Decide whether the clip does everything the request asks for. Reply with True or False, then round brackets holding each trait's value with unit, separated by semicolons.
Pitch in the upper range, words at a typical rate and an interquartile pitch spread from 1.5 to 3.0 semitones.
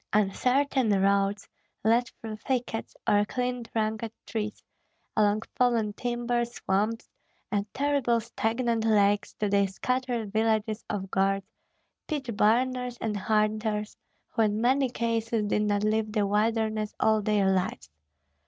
False (220 Hz; 125 wpm; 2.4 semitones)